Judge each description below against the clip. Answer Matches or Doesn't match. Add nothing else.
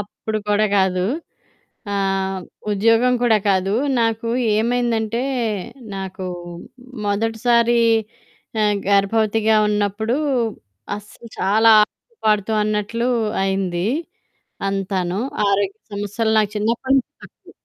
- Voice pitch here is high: Matches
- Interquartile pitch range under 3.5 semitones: Matches